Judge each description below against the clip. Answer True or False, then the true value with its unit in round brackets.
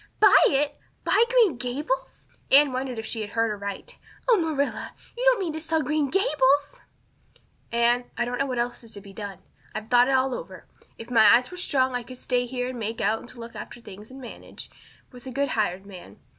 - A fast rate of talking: True (215 wpm)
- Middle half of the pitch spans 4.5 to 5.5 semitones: False (4.0 semitones)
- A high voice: True (250 Hz)